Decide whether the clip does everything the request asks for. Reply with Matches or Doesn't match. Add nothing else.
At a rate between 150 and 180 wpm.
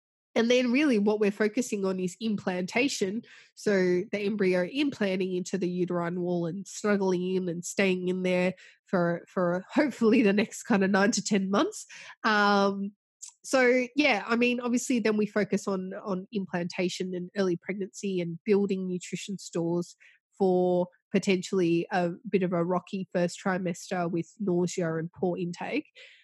Matches